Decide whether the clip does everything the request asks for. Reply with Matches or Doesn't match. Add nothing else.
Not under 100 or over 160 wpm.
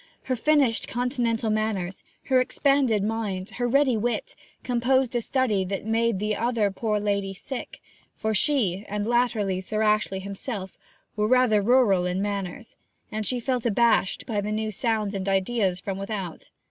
Matches